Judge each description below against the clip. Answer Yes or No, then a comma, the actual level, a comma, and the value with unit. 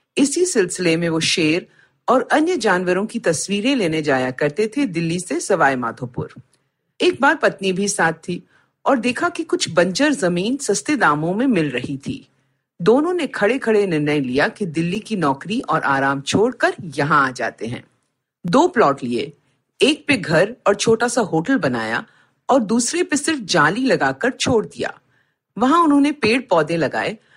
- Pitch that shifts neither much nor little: No, wide, 8.8 semitones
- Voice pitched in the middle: No, high, 200 Hz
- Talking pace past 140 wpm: Yes, average, 170 wpm